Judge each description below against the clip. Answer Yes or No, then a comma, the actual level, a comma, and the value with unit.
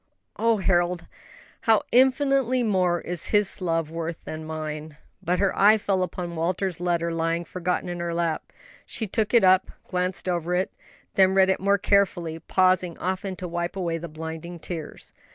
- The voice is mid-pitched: Yes, medium, 180 Hz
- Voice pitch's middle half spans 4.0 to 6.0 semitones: No, narrow, 2.4 semitones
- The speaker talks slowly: No, average, 175 wpm